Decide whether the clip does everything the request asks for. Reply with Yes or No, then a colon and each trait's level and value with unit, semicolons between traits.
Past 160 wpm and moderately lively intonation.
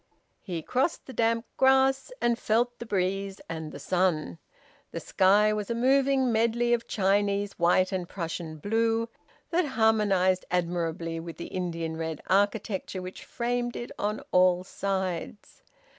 No: average, 145 wpm; average, 4.5 semitones